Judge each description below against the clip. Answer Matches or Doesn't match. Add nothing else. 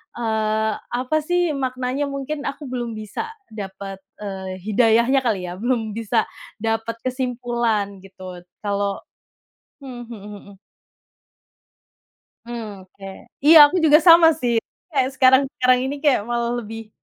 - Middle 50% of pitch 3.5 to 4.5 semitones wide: Matches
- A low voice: Doesn't match